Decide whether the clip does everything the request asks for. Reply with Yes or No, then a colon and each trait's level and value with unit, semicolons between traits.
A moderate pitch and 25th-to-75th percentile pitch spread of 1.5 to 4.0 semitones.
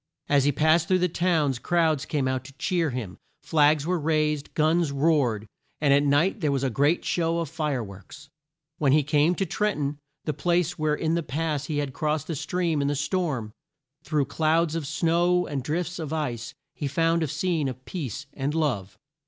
Yes: medium, 150 Hz; average, 3.0 semitones